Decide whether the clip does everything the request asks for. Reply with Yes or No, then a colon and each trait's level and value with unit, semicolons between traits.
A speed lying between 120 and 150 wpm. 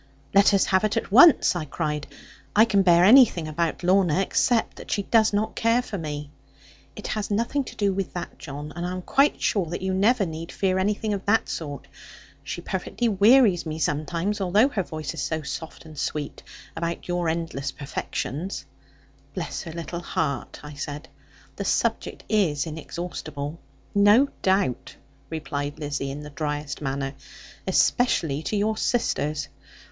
No: average, 165 wpm